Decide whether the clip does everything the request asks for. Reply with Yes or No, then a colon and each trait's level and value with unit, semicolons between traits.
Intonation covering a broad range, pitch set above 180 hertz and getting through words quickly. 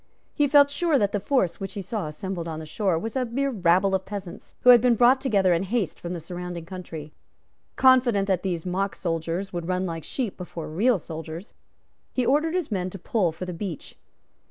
Yes: wide, 5.7 semitones; high, 190 Hz; fast, 210 wpm